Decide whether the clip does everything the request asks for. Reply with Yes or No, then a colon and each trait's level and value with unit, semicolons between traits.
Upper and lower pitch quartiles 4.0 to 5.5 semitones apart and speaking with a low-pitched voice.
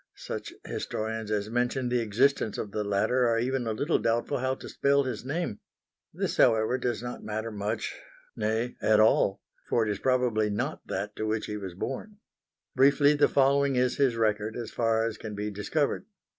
No: average, 3.4 semitones; low, 115 Hz